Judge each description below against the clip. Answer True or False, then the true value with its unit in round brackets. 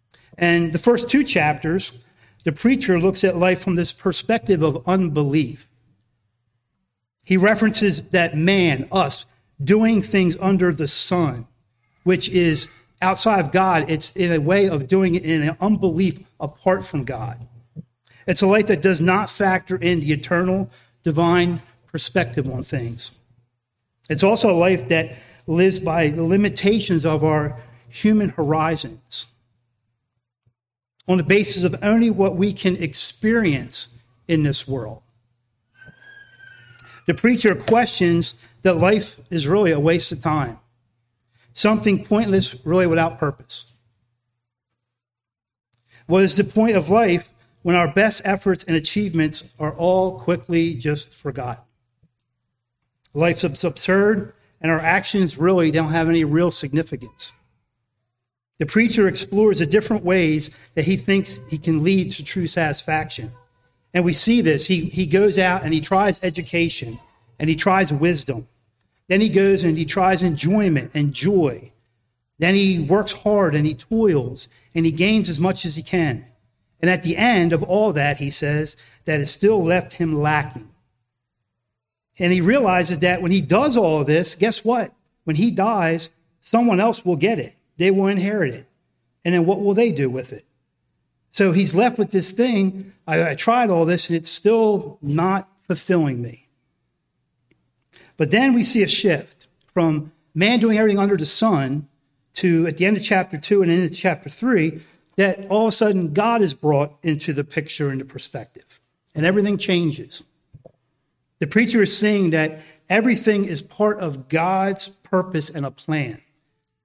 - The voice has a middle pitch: True (165 Hz)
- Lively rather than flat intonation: True (5.7 semitones)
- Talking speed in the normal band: True (155 wpm)